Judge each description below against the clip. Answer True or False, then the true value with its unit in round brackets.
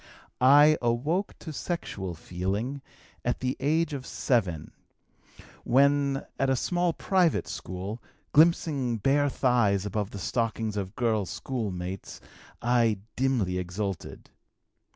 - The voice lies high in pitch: False (120 Hz)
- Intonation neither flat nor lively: False (6.0 semitones)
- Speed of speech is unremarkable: False (110 wpm)